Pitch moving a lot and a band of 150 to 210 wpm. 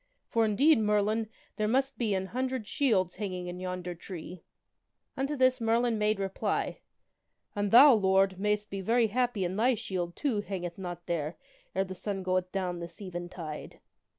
No: average, 3.8 semitones; average, 180 wpm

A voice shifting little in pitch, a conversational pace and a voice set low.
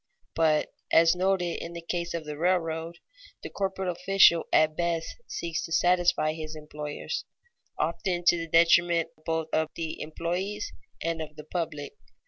No: narrow, 1.8 semitones; average, 150 wpm; medium, 165 Hz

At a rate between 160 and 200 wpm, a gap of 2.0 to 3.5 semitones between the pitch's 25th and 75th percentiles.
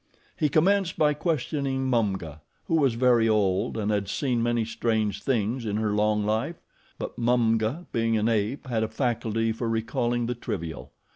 Yes: average, 165 wpm; average, 3.0 semitones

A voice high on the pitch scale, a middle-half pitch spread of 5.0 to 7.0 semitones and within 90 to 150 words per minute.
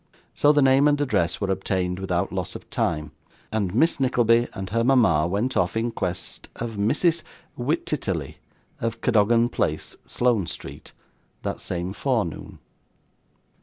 No: low, 110 Hz; wide, 5.6 semitones; average, 140 wpm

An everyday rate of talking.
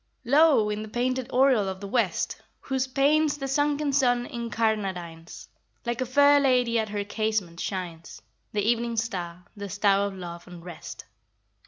Yes: average, 160 wpm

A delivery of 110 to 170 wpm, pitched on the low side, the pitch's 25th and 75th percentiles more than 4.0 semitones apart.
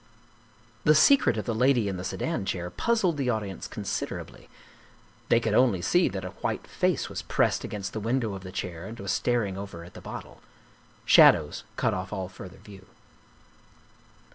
No: average, 180 wpm; low, 100 Hz; average, 4.5 semitones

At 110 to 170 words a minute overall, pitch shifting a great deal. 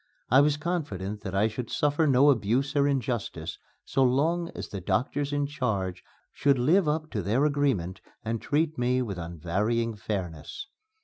Yes: average, 165 wpm; wide, 6.3 semitones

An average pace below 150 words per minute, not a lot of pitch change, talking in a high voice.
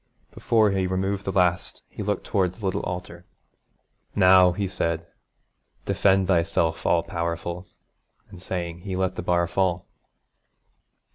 No: slow, 135 wpm; narrow, 1.8 semitones; very low, 90 Hz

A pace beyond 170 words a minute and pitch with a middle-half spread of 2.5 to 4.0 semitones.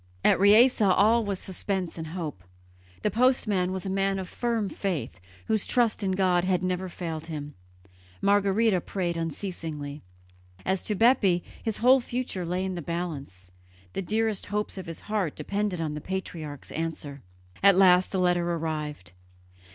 No: average, 160 wpm; average, 3.6 semitones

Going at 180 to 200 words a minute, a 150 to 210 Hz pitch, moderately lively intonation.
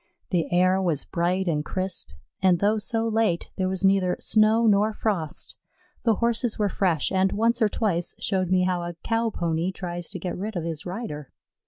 Yes: average, 190 wpm; high, 190 Hz; average, 3.6 semitones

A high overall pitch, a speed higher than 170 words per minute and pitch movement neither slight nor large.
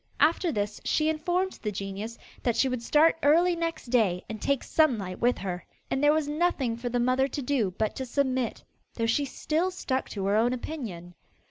No: very high, 255 Hz; average, 200 wpm; wide, 5.8 semitones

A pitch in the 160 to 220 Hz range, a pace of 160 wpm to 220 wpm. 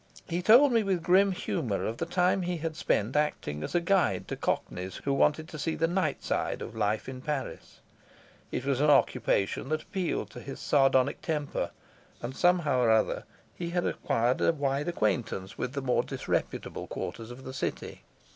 No: medium, 145 Hz; average, 185 wpm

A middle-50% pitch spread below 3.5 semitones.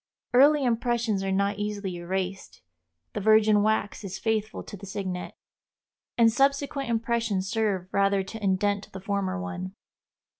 Yes: average, 2.7 semitones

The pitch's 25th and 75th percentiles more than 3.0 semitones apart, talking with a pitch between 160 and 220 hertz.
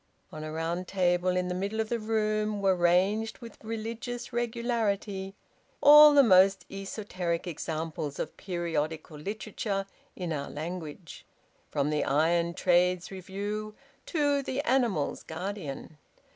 Yes: average, 4.3 semitones; high, 190 Hz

